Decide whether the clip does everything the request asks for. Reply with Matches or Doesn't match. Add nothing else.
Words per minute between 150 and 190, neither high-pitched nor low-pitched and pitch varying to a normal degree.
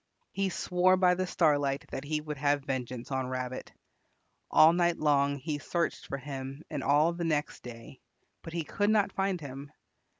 Matches